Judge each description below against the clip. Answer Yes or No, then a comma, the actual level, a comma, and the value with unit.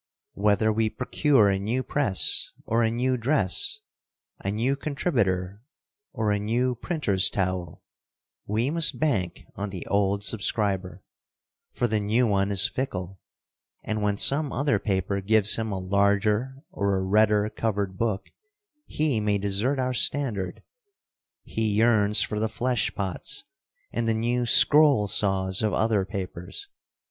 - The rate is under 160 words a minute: Yes, average, 140 wpm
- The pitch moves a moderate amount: Yes, average, 3.4 semitones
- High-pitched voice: No, low, 105 Hz